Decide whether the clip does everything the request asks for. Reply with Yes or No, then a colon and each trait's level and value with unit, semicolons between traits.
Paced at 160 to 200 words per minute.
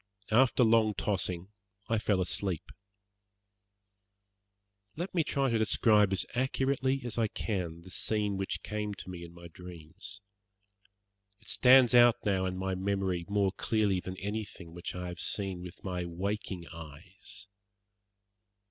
No: average, 140 wpm